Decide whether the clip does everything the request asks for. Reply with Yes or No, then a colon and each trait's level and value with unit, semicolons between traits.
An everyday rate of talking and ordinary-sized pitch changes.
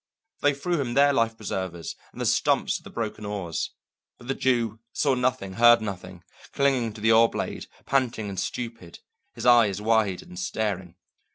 Yes: average, 175 wpm; average, 4.0 semitones